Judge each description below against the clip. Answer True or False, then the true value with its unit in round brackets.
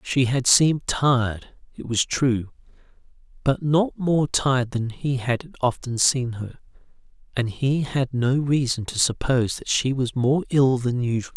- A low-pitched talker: True (130 Hz)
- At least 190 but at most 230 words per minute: False (165 wpm)